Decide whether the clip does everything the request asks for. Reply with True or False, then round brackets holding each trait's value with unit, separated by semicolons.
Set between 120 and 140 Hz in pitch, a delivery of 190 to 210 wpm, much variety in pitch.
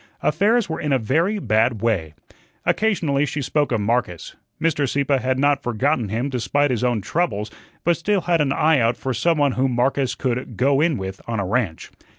False (135 Hz; 195 wpm; 4.5 semitones)